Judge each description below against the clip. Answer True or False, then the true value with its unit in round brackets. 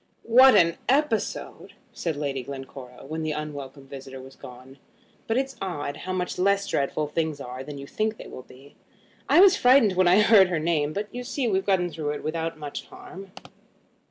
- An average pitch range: False (6.0 semitones)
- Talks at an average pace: True (190 wpm)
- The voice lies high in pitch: False (160 Hz)